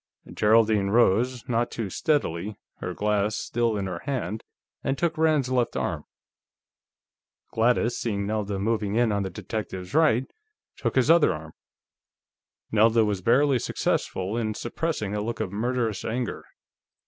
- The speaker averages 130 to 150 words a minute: Yes, average, 140 wpm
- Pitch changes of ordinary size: Yes, average, 3.3 semitones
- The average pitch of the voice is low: Yes, low, 110 Hz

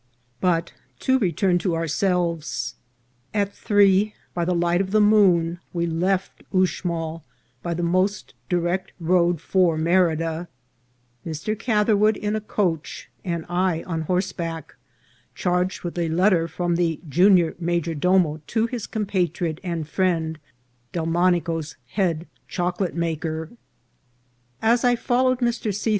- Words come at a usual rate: No, slow, 130 wpm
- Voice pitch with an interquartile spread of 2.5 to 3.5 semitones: Yes, average, 2.8 semitones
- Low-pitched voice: No, medium, 175 Hz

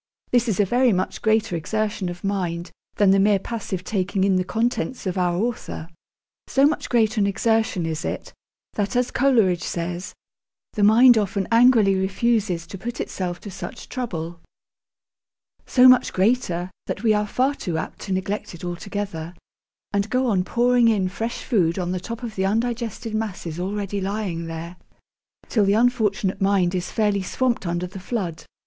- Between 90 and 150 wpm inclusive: No, average, 170 wpm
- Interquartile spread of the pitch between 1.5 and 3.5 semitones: No, average, 4.0 semitones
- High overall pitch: Yes, high, 200 Hz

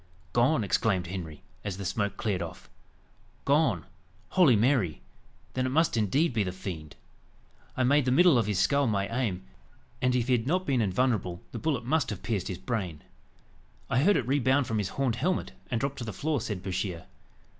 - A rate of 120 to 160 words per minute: No, average, 190 wpm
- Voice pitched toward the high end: No, low, 115 Hz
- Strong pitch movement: Yes, wide, 6.1 semitones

